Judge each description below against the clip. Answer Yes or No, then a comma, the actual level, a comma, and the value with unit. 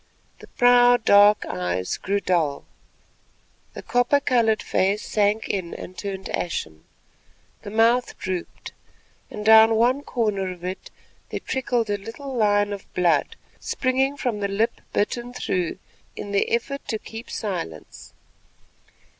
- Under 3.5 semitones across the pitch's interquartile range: No, average, 4.1 semitones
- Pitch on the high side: Yes, high, 210 Hz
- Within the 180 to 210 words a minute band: No, slow, 135 wpm